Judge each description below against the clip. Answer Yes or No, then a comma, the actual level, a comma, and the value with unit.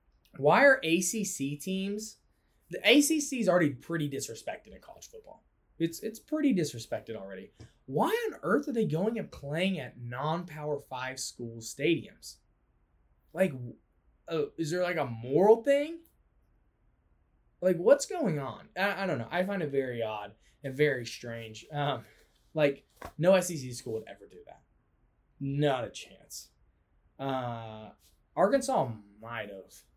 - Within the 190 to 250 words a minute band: No, average, 140 wpm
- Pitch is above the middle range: No, medium, 145 Hz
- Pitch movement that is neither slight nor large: No, wide, 8.5 semitones